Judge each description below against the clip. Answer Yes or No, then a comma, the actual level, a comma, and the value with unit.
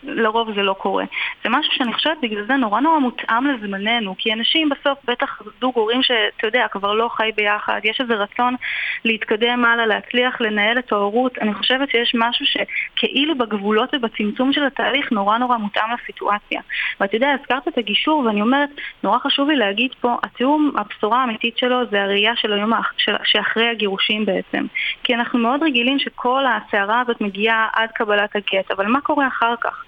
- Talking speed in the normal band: No, fast, 175 wpm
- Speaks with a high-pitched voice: Yes, high, 235 Hz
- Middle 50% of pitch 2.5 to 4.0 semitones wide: Yes, average, 3.7 semitones